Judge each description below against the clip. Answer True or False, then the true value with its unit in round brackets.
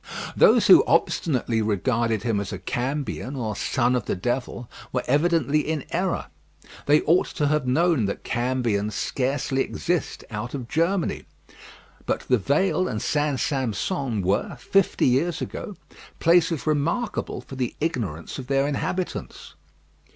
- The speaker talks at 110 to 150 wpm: True (140 wpm)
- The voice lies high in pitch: False (135 Hz)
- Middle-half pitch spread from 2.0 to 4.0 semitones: False (4.9 semitones)